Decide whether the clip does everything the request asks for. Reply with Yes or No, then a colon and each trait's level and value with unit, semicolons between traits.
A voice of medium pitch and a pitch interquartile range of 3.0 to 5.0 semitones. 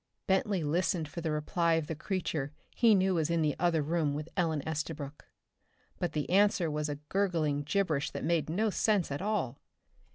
Yes: medium, 165 Hz; average, 3.7 semitones